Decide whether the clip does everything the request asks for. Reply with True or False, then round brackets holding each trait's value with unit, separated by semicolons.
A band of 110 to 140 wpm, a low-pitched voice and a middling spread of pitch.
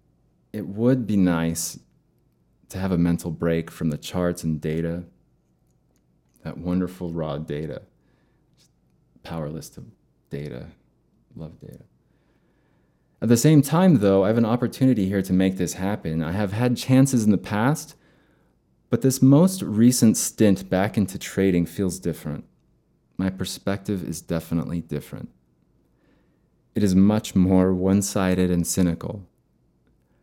True (135 wpm; 95 Hz; 4.3 semitones)